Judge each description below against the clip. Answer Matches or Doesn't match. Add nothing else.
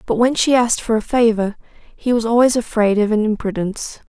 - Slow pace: Doesn't match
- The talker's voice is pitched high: Matches